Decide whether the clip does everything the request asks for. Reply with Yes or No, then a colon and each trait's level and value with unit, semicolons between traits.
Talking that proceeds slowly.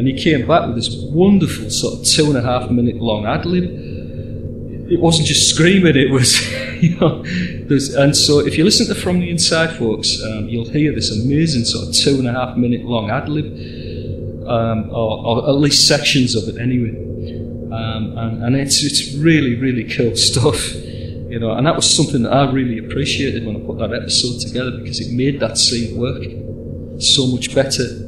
No: average, 200 wpm